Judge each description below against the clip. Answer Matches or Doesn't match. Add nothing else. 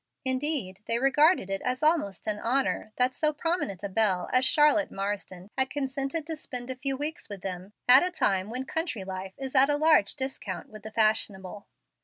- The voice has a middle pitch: Doesn't match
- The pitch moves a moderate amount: Doesn't match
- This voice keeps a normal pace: Matches